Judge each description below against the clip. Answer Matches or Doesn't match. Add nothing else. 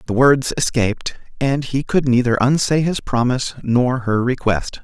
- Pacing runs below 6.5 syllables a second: Matches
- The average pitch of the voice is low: Matches